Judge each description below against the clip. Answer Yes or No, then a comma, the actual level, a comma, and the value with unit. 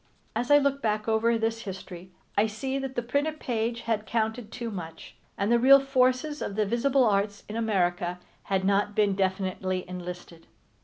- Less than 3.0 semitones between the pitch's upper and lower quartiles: No, average, 4.2 semitones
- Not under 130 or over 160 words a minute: No, average, 175 wpm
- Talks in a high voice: Yes, high, 220 Hz